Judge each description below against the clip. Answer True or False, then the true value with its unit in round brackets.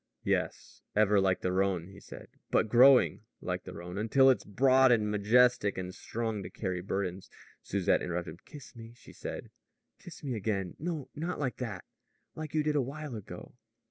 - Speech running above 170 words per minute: True (185 wpm)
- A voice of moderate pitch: False (110 Hz)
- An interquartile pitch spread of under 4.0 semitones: False (5.5 semitones)